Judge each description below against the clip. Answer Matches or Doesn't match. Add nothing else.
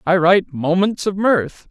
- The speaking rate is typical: Matches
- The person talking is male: Matches